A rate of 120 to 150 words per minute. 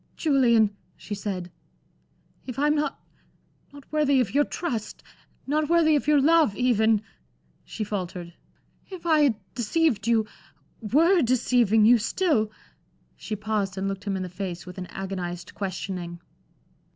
Yes: average, 140 wpm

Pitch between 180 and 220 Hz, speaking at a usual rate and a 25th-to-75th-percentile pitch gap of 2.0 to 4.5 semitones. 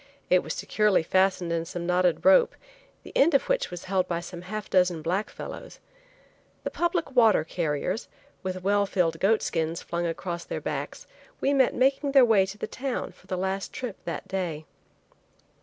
No: high, 190 Hz; average, 180 wpm; average, 4.9 semitones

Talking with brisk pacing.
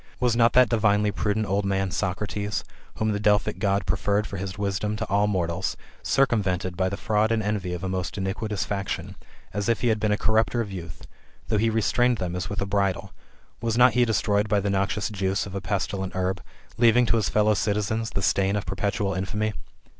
Yes: fast, 210 wpm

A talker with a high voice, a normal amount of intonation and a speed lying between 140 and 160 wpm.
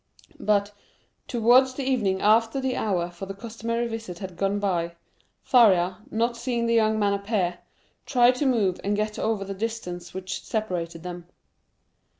Yes: high, 210 Hz; average, 3.6 semitones; average, 155 wpm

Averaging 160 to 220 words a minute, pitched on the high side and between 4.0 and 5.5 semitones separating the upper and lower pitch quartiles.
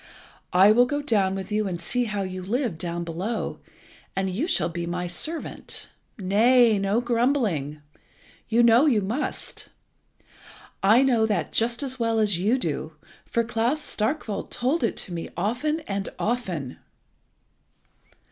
No: average, 145 wpm; high, 215 Hz; average, 4.7 semitones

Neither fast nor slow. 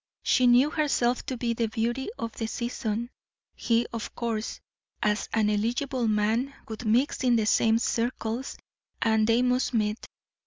Yes: average, 155 wpm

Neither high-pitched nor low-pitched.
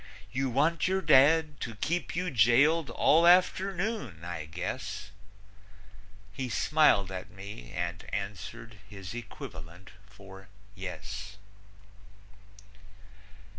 No: low, 115 Hz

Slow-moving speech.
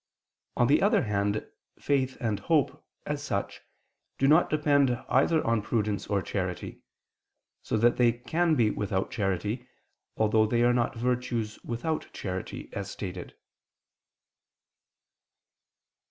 Yes: slow, 125 wpm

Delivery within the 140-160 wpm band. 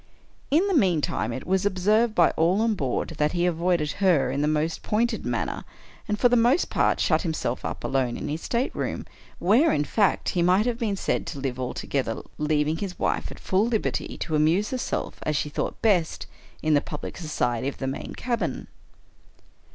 No: average, 190 wpm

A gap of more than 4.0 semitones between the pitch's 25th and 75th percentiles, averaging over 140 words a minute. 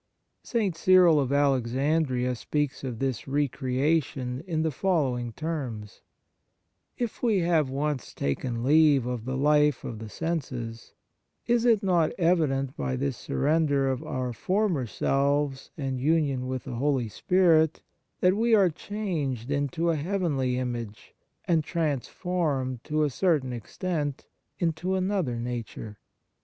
No: average, 4.7 semitones; slow, 135 wpm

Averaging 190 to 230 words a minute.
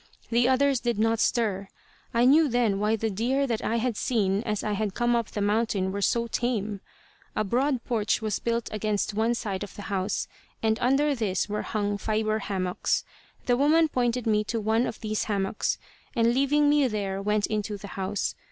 Yes: average, 195 wpm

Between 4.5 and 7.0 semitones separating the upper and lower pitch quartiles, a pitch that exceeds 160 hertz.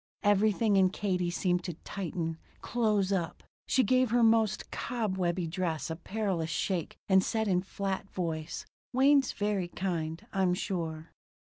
No: average, 3.5 semitones; high, 190 Hz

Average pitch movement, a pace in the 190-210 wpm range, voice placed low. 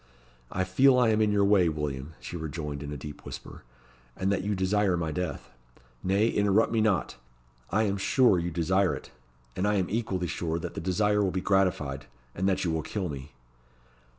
Yes: average, 4.0 semitones; average, 200 wpm; very low, 95 Hz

